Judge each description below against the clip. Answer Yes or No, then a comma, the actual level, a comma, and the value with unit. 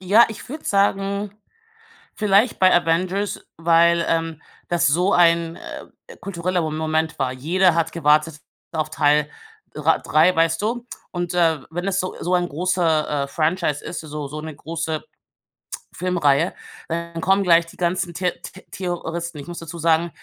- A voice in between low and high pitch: Yes, medium, 170 Hz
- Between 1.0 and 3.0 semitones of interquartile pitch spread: Yes, narrow, 2.4 semitones